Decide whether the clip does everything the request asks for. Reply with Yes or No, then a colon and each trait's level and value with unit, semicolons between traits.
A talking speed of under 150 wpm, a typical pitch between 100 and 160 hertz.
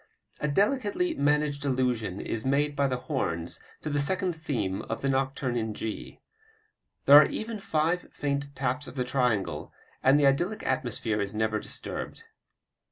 No: average, 160 wpm; medium, 140 Hz